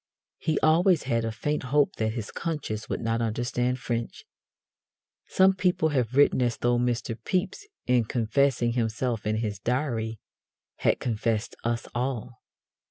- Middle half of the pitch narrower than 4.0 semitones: Yes, average, 3.6 semitones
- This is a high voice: No, low, 120 Hz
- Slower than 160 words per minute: Yes, average, 145 wpm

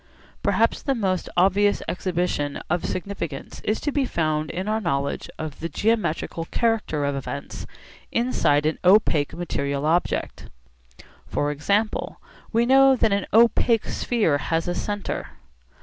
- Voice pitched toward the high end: No, medium, 180 Hz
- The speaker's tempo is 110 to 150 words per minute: Yes, slow, 135 wpm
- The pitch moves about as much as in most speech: No, wide, 6.2 semitones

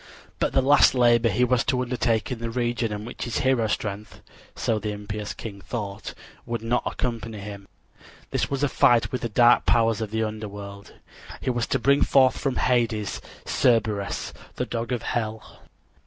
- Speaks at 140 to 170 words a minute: No, average, 180 wpm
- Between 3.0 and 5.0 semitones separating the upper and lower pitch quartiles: No, narrow, 2.5 semitones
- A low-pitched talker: Yes, low, 115 Hz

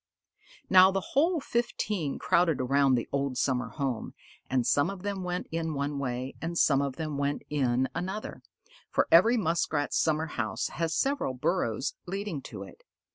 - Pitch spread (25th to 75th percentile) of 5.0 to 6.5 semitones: Yes, wide, 5.4 semitones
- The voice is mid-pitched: Yes, medium, 155 Hz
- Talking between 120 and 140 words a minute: No, average, 165 wpm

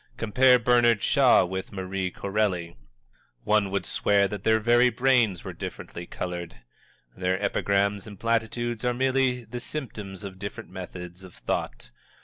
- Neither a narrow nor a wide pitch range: Yes, average, 4.1 semitones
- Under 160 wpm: Yes, average, 140 wpm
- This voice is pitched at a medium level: No, low, 105 Hz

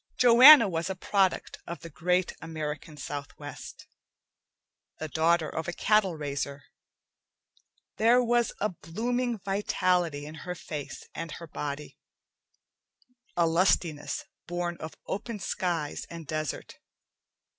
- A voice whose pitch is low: No, medium, 170 Hz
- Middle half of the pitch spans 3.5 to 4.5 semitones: Yes, average, 4.2 semitones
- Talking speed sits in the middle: No, slow, 115 wpm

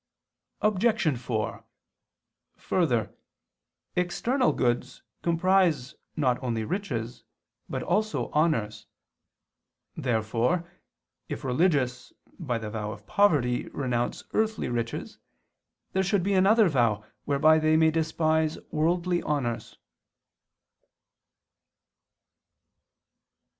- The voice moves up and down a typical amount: No, wide, 6.9 semitones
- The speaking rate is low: Yes, slow, 85 wpm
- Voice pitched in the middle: Yes, medium, 155 Hz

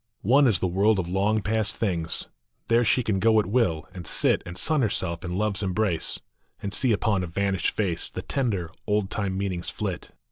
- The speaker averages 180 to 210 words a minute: Yes, fast, 205 wpm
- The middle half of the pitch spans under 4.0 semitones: Yes, average, 3.3 semitones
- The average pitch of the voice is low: Yes, low, 100 Hz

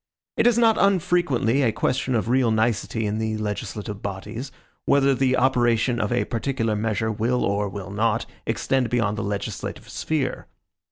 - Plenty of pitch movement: No, average, 3.8 semitones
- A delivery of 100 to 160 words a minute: Yes, average, 155 wpm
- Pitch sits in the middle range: No, low, 115 Hz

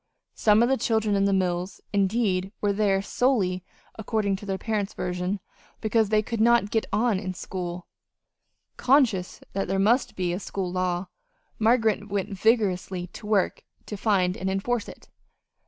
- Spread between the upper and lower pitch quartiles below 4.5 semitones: Yes, average, 2.9 semitones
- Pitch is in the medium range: No, high, 200 Hz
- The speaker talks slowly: No, average, 160 wpm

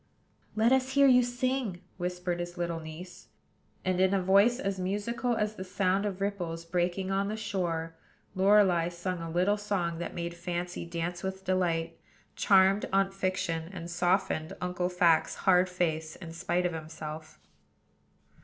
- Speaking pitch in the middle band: Yes, medium, 180 Hz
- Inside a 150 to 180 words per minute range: Yes, average, 155 wpm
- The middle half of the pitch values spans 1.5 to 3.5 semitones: Yes, narrow, 2.4 semitones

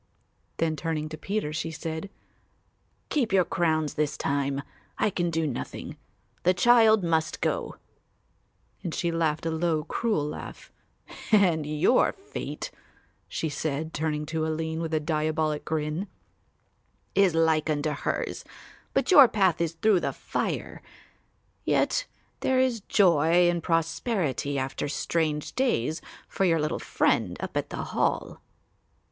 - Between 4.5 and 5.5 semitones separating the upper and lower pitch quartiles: No, average, 3.0 semitones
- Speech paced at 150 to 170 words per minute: No, slow, 135 wpm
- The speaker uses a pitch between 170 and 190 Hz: No, medium, 160 Hz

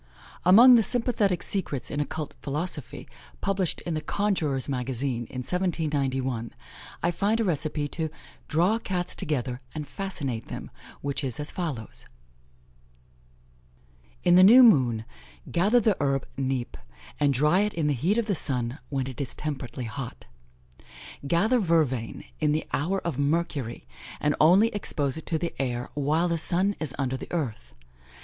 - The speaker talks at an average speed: Yes, average, 150 wpm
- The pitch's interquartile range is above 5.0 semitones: Yes, wide, 5.4 semitones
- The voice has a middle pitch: Yes, medium, 150 Hz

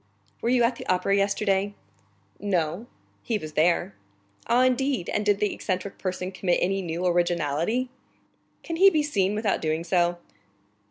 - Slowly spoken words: No, average, 155 wpm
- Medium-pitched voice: No, high, 195 Hz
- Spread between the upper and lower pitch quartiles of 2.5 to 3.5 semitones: No, average, 4.7 semitones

